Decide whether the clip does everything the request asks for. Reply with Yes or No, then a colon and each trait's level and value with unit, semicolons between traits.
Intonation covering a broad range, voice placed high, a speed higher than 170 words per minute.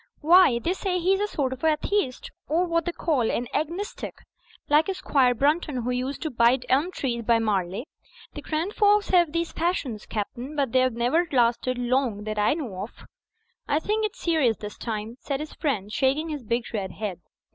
Yes: wide, 6.0 semitones; very high, 270 Hz; average, 190 wpm